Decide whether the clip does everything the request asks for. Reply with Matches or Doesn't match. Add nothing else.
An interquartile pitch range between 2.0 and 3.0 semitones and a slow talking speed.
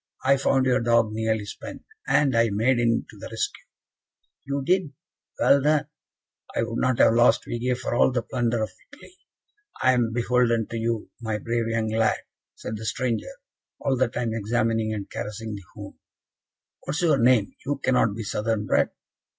Doesn't match